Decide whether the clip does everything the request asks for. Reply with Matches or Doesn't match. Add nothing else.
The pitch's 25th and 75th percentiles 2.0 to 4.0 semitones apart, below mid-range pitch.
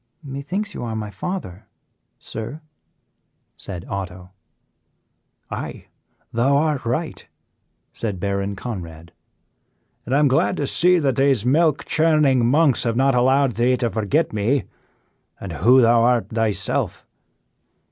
Doesn't match